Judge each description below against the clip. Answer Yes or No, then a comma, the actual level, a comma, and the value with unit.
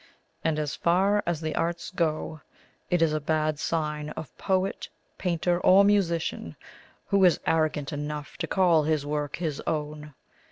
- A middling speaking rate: Yes, average, 155 wpm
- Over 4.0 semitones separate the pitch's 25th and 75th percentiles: No, narrow, 2.6 semitones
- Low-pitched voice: No, medium, 160 Hz